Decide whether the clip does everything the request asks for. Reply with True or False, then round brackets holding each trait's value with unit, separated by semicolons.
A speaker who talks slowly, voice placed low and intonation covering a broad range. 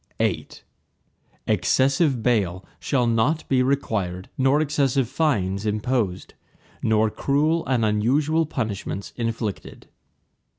False (95 wpm; 120 Hz; 4.8 semitones)